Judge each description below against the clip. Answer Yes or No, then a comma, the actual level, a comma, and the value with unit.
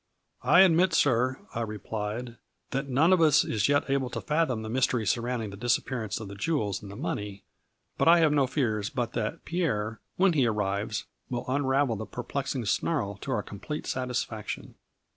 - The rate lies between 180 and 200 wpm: Yes, average, 185 wpm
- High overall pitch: No, low, 125 Hz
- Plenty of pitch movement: No, average, 4.9 semitones